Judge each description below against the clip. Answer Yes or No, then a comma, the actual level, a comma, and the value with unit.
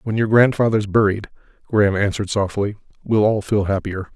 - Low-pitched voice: Yes, low, 105 Hz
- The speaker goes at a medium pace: Yes, average, 160 wpm